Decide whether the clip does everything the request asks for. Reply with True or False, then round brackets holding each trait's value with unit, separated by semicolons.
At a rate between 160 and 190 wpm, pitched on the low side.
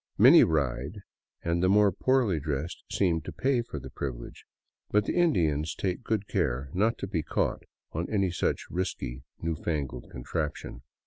True (165 wpm; 85 Hz)